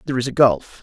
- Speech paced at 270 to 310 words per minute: Yes, fast, 290 wpm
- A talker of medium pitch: No, low, 125 Hz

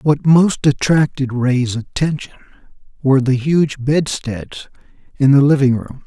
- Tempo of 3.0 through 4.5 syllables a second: Yes, 4.1 syllables/s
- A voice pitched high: No, low, 135 Hz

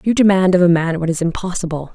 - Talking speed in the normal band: No, fast, 245 wpm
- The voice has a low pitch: No, medium, 175 Hz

